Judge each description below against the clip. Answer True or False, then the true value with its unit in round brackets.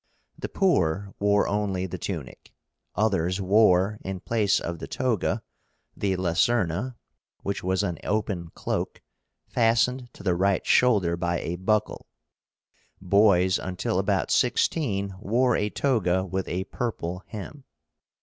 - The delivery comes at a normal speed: False (130 wpm)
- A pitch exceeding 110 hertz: False (100 Hz)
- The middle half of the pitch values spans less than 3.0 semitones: False (3.3 semitones)